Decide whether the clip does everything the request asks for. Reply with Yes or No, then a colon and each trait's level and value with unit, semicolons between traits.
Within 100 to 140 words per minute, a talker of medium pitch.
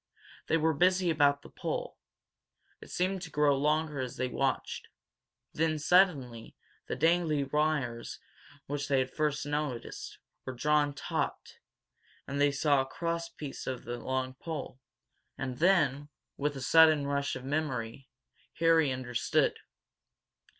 Yes: slow, 135 wpm; medium, 145 Hz